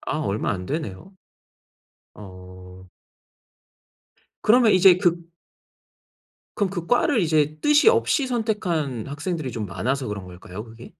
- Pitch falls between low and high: Yes, medium, 150 Hz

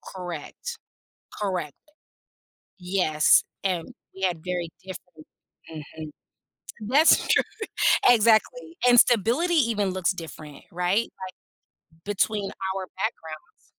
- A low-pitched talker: No, high, 190 Hz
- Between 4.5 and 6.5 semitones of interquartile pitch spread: Yes, average, 4.9 semitones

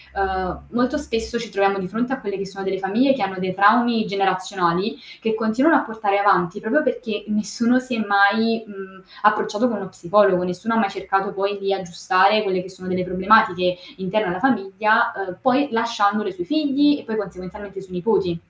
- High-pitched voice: Yes, high, 200 Hz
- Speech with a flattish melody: No, average, 3.0 semitones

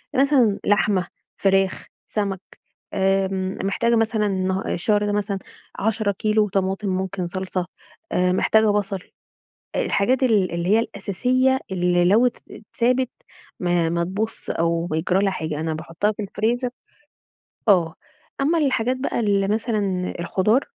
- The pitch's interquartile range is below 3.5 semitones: Yes, average, 3.0 semitones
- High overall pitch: Yes, high, 200 Hz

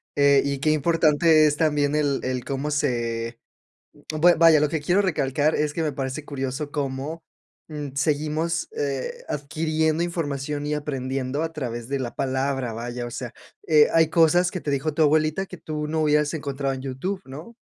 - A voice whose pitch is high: No, medium, 150 Hz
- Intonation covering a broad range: No, average, 2.7 semitones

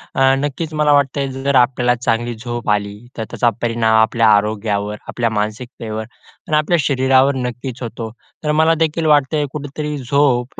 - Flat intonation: No, average, 4.2 semitones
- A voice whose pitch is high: No, low, 125 Hz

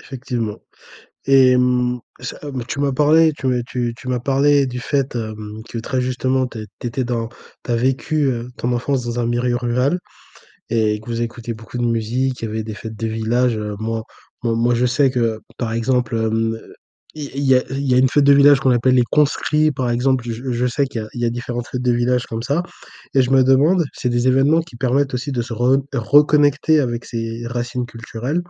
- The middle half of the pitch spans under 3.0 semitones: Yes, narrow, 2.4 semitones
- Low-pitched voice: Yes, low, 125 Hz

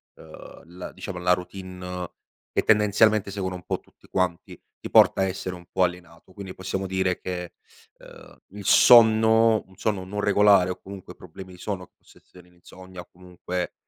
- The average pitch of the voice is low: Yes, very low, 95 Hz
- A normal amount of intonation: No, narrow, 1.9 semitones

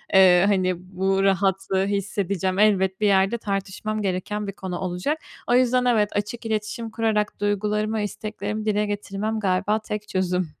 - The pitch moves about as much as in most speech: No, narrow, 2.0 semitones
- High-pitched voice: Yes, high, 205 Hz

